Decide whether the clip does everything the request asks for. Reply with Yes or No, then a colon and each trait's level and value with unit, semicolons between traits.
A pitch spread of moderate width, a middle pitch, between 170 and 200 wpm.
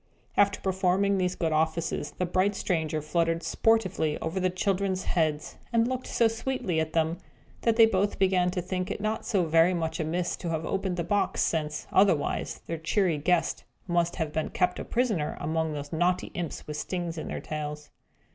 Yes: average, 3.2 semitones; medium, 175 Hz; average, 185 wpm